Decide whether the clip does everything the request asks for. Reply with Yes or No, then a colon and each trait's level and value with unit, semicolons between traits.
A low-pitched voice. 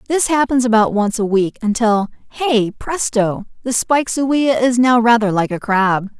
No: high, 230 Hz